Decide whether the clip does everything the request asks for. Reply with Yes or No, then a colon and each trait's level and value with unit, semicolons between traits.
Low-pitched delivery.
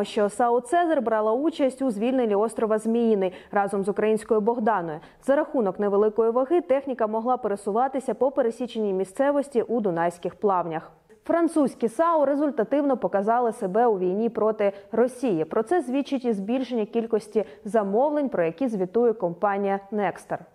No: high, 225 Hz